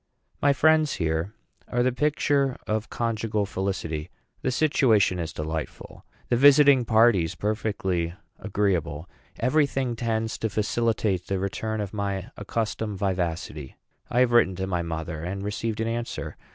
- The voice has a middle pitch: No, low, 105 Hz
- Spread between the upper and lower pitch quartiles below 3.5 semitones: No, average, 4.5 semitones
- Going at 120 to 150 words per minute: Yes, average, 140 wpm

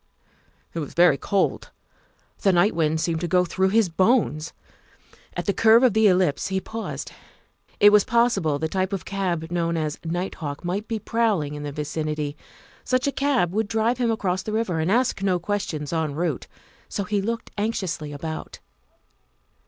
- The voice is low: No, medium, 185 Hz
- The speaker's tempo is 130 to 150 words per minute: No, average, 175 wpm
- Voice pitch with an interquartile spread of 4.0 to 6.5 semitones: Yes, average, 5.2 semitones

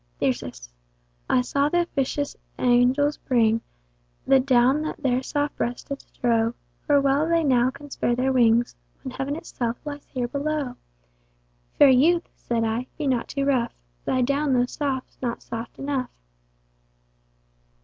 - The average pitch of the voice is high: Yes, very high, 265 Hz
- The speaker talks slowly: No, average, 145 wpm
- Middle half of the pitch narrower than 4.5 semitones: Yes, average, 2.9 semitones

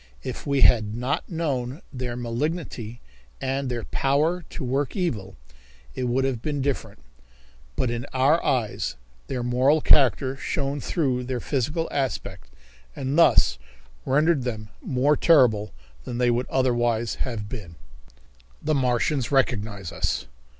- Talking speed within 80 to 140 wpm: Yes, slow, 135 wpm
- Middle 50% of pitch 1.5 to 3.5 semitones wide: Yes, average, 2.9 semitones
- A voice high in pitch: No, low, 130 Hz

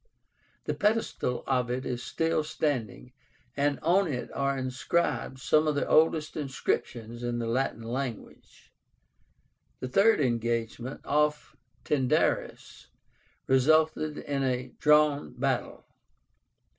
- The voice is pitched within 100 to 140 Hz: Yes, low, 135 Hz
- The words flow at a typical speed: No, slow, 110 wpm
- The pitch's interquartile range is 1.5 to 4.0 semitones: Yes, average, 3.5 semitones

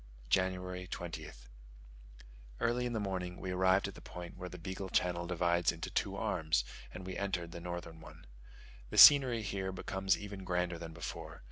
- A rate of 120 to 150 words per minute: No, average, 170 wpm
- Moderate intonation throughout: No, narrow, 1.8 semitones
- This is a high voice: No, very low, 90 Hz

